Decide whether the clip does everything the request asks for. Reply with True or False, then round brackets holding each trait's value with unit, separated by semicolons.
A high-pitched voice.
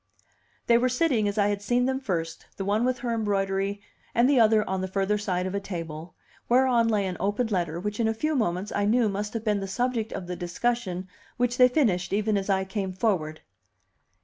True (205 Hz)